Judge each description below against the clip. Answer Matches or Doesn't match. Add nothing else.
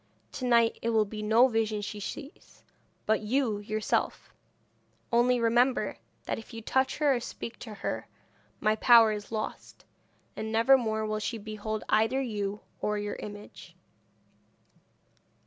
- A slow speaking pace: Doesn't match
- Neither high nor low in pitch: Doesn't match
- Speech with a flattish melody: Matches